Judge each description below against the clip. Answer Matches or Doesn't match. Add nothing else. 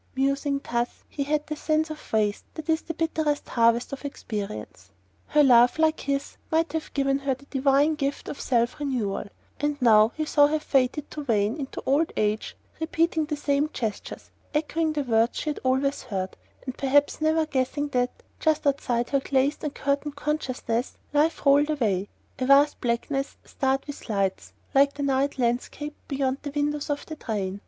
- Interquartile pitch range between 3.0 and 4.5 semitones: Matches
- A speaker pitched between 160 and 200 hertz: Doesn't match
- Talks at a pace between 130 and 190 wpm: Matches